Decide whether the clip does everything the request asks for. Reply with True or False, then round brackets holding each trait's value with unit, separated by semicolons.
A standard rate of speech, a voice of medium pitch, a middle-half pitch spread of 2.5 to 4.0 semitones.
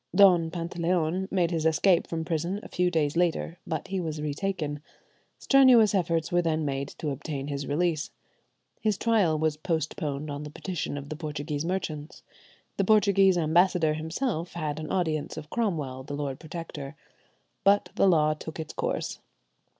True (160 wpm; 160 Hz; 3.1 semitones)